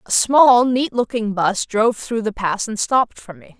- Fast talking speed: Yes, fast, 215 wpm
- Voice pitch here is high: Yes, high, 220 Hz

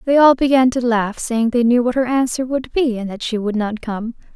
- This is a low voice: No, high, 240 Hz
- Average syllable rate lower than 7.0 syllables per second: Yes, 5.2 syllables/s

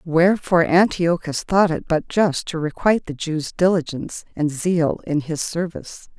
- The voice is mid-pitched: Yes, medium, 165 Hz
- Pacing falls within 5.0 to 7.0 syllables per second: No, 4.8 syllables/s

